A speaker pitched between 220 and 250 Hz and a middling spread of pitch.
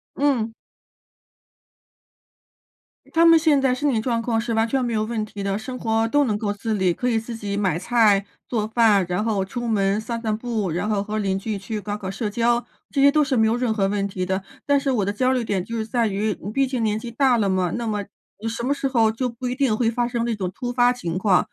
Yes: high, 225 Hz; average, 3.1 semitones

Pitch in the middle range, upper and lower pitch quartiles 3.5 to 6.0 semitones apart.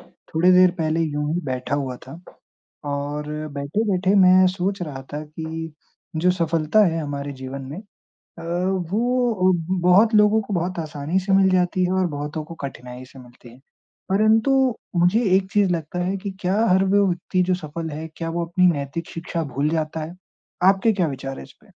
Yes: medium, 170 Hz; average, 4.2 semitones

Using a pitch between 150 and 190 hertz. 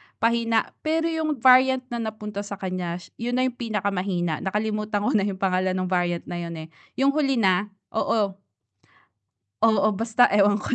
No: high, 210 Hz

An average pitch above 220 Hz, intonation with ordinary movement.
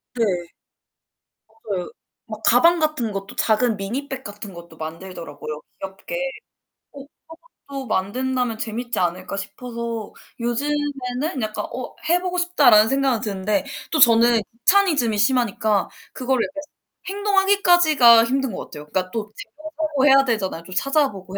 No: high, 235 Hz; wide, 5.7 semitones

